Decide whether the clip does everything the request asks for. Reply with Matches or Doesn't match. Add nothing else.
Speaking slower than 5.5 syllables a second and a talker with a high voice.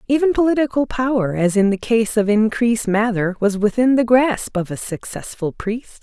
Matches